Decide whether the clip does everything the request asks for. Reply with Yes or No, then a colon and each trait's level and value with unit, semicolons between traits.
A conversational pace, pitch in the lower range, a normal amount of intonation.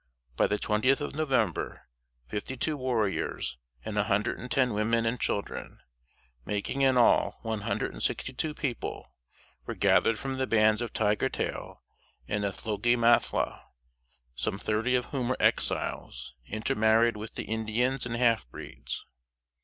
Yes: average, 150 wpm; low, 115 Hz; average, 3.1 semitones